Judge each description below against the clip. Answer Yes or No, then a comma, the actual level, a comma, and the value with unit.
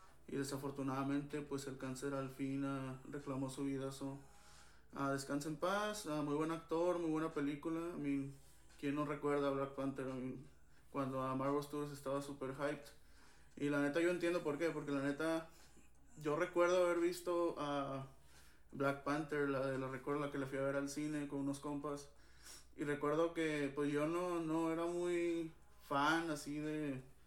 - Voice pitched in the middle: Yes, medium, 145 Hz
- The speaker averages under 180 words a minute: No, fast, 190 wpm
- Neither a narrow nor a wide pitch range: No, narrow, 2.1 semitones